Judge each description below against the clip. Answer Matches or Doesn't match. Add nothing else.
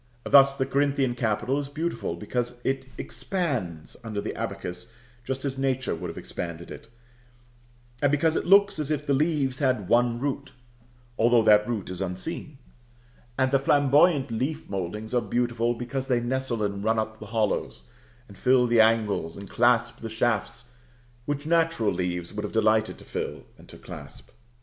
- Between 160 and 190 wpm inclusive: Matches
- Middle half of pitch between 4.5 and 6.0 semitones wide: Doesn't match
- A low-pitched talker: Matches